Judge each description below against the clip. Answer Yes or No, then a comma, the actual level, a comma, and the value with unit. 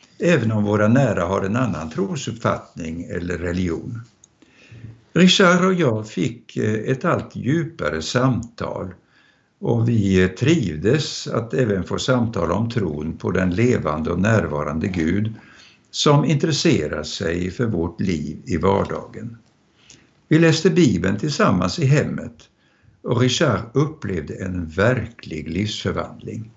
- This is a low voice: Yes, low, 110 Hz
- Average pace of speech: No, slow, 120 wpm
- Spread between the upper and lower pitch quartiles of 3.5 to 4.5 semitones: No, average, 5.3 semitones